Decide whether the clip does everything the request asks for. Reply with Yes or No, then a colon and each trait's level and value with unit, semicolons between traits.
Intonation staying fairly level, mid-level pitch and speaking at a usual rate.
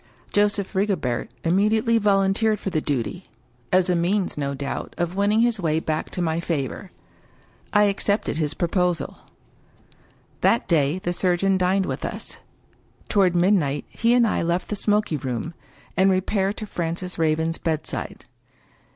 No: average, 3.9 semitones; medium, 180 Hz; average, 160 wpm